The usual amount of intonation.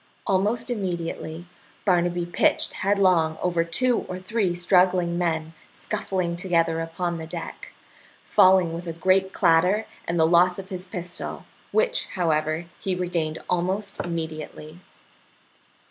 No: narrow, 2.2 semitones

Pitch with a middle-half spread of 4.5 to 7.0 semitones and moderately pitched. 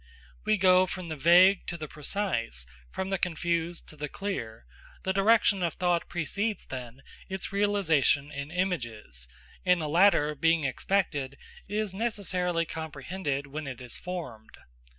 Yes: average, 5.0 semitones; medium, 170 Hz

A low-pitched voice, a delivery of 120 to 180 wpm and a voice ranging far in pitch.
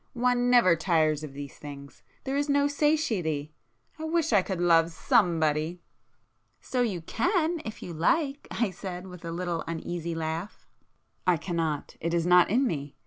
No: medium, 175 Hz; average, 155 wpm; wide, 7.1 semitones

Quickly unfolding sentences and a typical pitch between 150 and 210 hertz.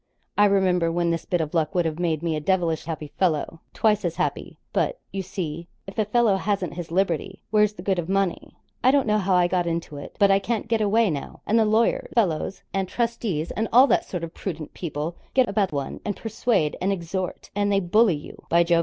Yes: fast, 230 wpm; medium, 185 Hz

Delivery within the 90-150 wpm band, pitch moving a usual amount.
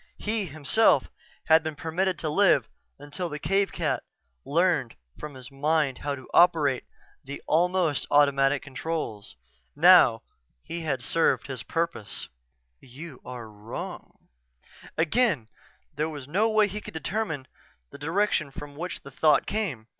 Yes: average, 140 wpm; average, 4.4 semitones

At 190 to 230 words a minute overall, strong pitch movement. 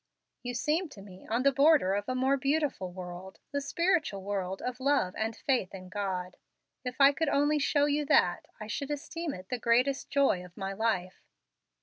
Yes: average, 195 wpm; wide, 6.8 semitones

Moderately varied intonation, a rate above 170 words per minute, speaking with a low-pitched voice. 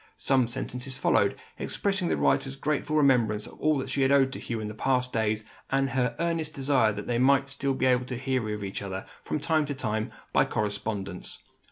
Yes: average, 4.2 semitones; average, 190 wpm; low, 130 Hz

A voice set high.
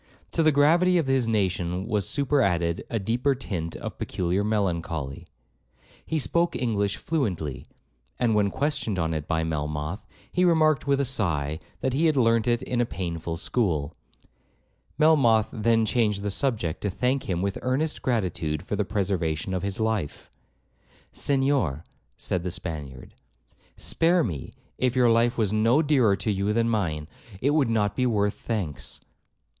No: low, 105 Hz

